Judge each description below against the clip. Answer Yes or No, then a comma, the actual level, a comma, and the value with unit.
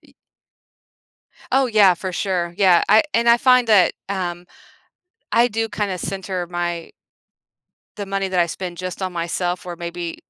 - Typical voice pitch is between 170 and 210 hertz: Yes, medium, 185 Hz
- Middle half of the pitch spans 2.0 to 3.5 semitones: Yes, average, 3.0 semitones